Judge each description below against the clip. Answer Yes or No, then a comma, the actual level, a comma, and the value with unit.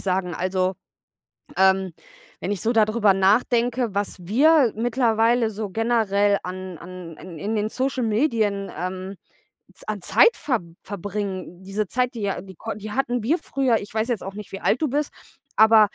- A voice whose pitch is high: Yes, high, 210 Hz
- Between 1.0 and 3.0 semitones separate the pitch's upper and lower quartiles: No, average, 3.6 semitones